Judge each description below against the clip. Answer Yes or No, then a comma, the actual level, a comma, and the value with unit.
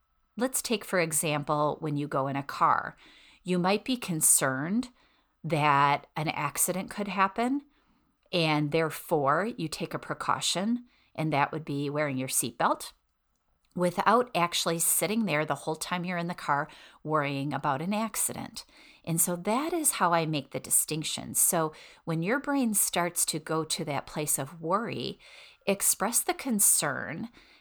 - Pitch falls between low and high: Yes, medium, 165 Hz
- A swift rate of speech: No, average, 155 wpm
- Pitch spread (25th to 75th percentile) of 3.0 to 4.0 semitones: No, wide, 5.4 semitones